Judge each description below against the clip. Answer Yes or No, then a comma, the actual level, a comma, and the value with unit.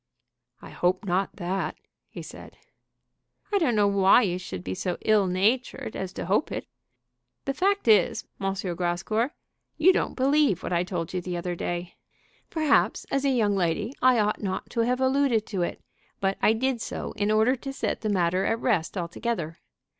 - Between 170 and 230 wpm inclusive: Yes, average, 185 wpm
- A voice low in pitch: No, high, 205 Hz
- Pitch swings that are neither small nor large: No, wide, 5.7 semitones